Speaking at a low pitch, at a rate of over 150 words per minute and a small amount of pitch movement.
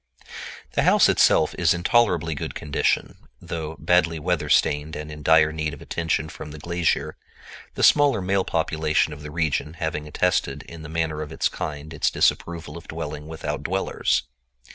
Yes: very low, 80 Hz; average, 170 wpm; narrow, 1.8 semitones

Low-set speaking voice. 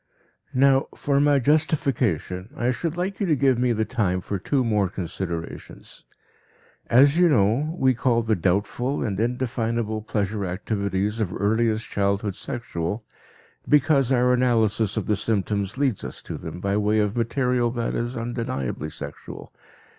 Yes: low, 115 Hz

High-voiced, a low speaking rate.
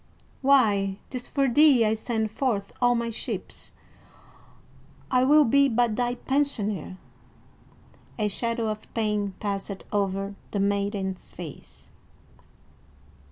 Yes: high, 220 Hz; slow, 115 wpm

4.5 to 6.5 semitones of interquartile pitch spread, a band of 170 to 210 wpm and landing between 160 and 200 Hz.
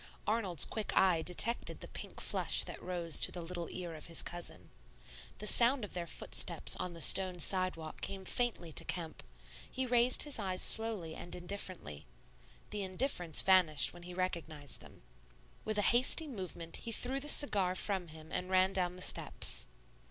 No: average, 3.8 semitones; average, 175 wpm; medium, 185 Hz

